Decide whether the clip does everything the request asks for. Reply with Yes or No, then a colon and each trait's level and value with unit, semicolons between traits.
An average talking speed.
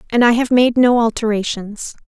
Yes: average, 175 wpm